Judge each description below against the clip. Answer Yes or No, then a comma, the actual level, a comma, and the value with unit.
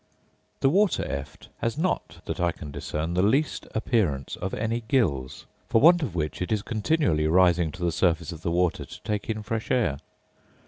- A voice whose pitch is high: No, very low, 90 Hz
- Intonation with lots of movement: Yes, wide, 6.0 semitones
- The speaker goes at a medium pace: Yes, average, 190 wpm